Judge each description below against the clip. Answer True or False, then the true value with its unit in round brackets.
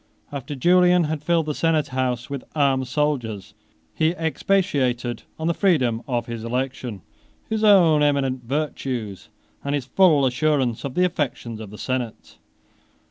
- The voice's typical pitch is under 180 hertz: True (140 Hz)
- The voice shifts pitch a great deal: False (4.4 semitones)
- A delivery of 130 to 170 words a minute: True (150 wpm)